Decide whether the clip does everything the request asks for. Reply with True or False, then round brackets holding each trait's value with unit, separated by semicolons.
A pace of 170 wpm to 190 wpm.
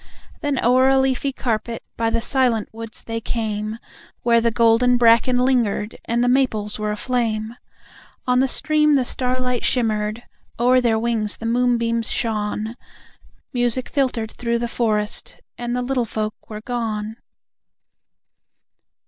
False (140 wpm)